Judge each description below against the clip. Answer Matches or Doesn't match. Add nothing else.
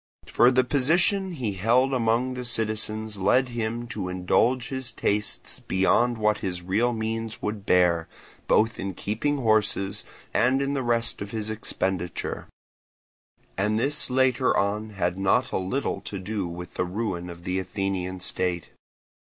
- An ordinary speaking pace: Matches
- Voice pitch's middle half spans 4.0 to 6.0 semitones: Matches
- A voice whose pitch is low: Matches